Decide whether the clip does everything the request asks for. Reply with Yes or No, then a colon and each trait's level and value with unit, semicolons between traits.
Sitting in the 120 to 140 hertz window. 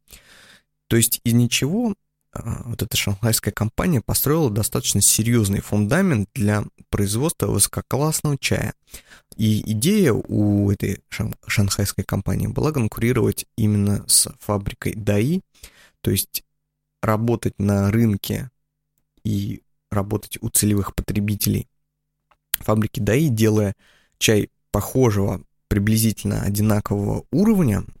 No: low, 110 Hz